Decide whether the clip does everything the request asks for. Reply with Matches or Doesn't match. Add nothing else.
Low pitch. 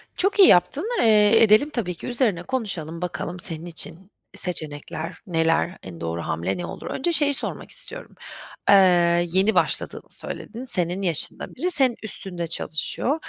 Doesn't match